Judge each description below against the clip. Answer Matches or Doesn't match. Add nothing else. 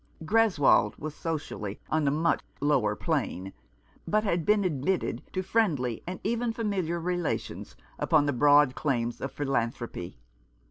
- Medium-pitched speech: Matches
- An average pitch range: Doesn't match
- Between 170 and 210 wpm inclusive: Doesn't match